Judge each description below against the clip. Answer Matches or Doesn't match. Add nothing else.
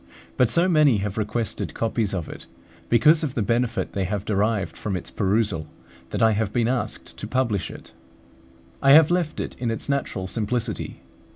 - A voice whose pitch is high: Doesn't match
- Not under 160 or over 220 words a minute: Matches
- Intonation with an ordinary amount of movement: Matches